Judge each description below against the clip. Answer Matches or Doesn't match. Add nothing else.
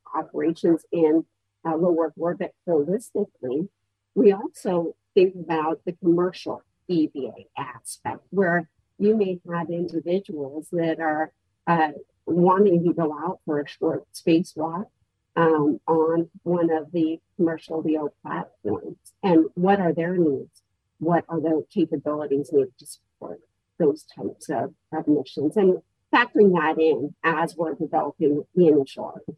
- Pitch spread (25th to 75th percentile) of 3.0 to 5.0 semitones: Doesn't match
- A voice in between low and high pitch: Matches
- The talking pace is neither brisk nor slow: Doesn't match